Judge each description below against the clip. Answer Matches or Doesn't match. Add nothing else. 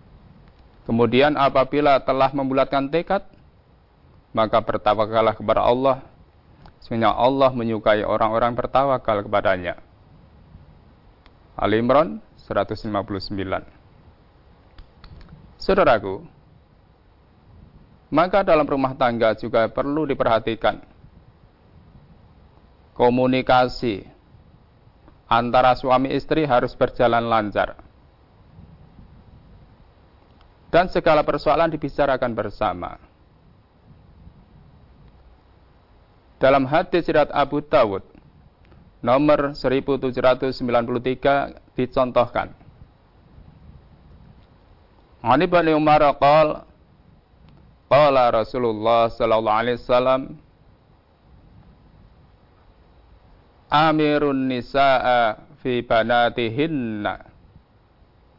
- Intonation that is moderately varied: Doesn't match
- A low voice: Matches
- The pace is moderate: Doesn't match